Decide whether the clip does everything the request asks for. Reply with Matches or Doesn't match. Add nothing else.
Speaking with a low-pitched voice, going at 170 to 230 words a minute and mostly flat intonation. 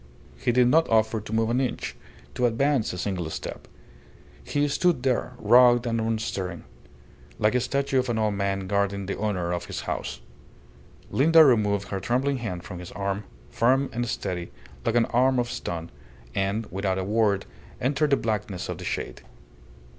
Doesn't match